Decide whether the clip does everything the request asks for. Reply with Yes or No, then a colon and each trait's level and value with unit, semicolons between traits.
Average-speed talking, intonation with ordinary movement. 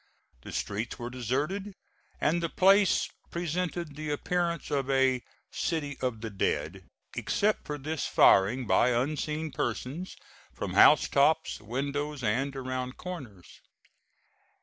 No: slow, 125 wpm; average, 4.7 semitones